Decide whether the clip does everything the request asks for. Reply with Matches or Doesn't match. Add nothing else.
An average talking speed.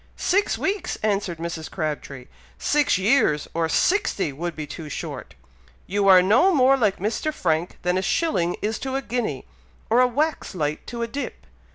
Matches